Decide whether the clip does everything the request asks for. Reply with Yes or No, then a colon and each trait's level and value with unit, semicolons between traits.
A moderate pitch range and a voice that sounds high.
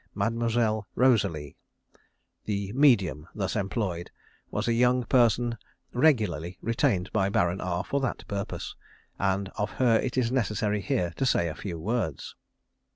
No: average, 4.2 semitones; low, 105 Hz